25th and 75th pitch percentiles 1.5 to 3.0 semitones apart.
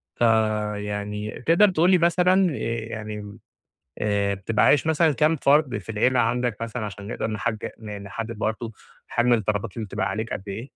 No: average, 4.2 semitones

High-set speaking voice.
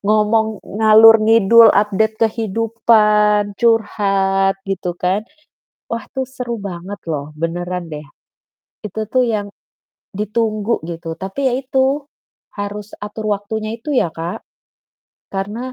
Yes: high, 210 Hz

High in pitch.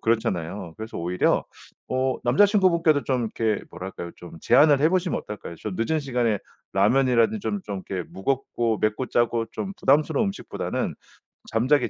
No: low, 120 Hz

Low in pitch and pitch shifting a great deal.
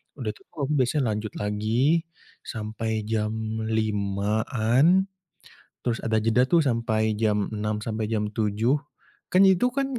No: low, 110 Hz; average, 3.1 semitones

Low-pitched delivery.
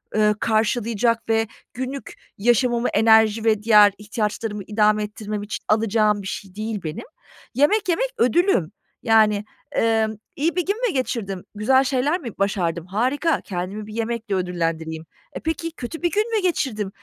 No: high, 220 Hz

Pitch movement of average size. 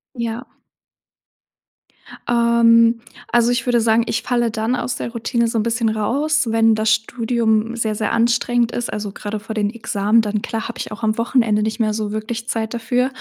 No: narrow, 1.4 semitones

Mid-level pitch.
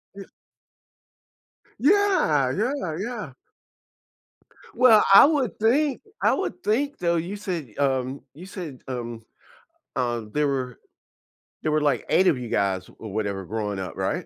Yes: medium, 155 Hz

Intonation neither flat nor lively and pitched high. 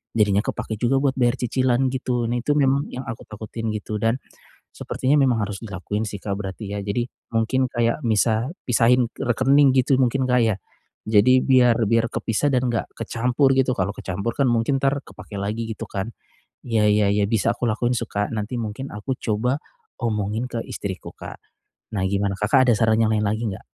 No: average, 3.1 semitones; low, 115 Hz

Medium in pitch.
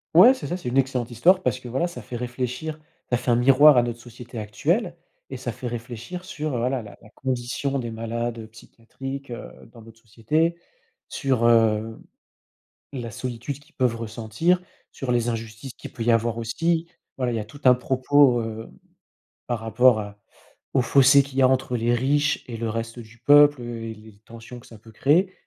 No: low, 120 Hz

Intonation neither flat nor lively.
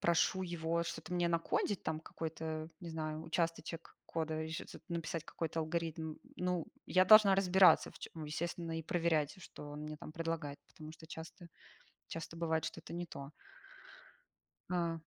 No: narrow, 1.4 semitones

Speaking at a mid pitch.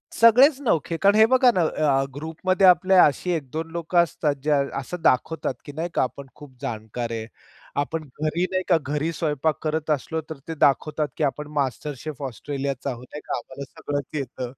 Yes: medium, 150 Hz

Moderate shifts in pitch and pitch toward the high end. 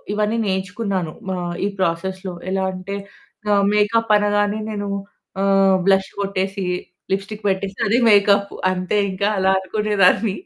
No: narrow, 1.5 semitones; high, 195 Hz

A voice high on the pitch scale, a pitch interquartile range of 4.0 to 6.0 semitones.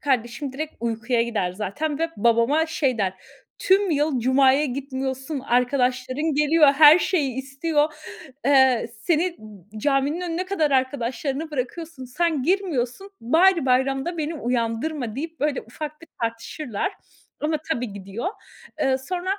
Yes: very high, 275 Hz; average, 4.4 semitones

